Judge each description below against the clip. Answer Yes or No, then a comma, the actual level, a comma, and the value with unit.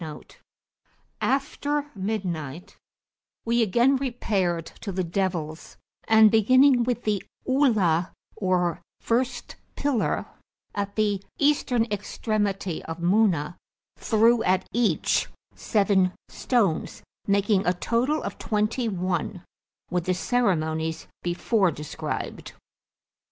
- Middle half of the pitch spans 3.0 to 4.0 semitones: No, average, 4.9 semitones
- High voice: Yes, high, 205 Hz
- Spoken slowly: Yes, slow, 100 wpm